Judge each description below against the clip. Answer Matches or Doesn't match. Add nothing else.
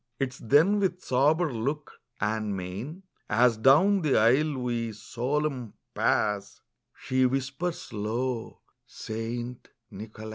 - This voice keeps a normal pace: Doesn't match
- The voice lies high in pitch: Doesn't match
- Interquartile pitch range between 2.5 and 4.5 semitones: Doesn't match